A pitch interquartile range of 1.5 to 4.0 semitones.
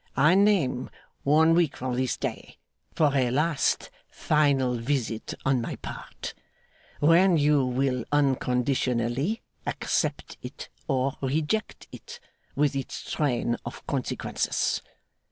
Yes: average, 3.3 semitones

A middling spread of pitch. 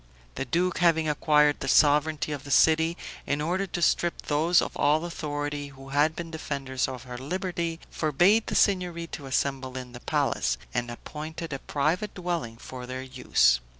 Yes: average, 4.1 semitones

